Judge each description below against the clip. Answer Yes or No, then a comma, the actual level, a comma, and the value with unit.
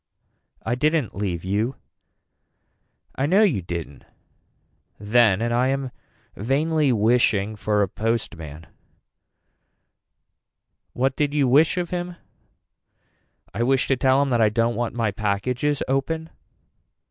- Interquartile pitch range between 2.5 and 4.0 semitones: No, average, 4.9 semitones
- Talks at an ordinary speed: No, slow, 125 wpm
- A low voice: Yes, low, 120 Hz